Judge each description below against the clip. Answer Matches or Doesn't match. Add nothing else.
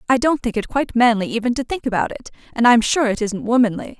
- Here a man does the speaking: Doesn't match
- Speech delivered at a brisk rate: Matches